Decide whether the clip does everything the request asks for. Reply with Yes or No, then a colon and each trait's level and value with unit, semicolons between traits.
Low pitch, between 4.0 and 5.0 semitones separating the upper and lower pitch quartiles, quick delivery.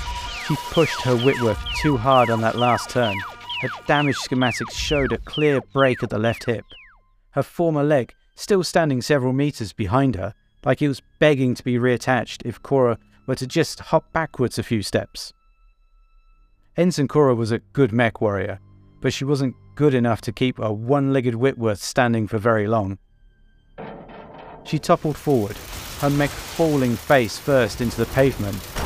No: low, 130 Hz; average, 4.5 semitones; average, 170 wpm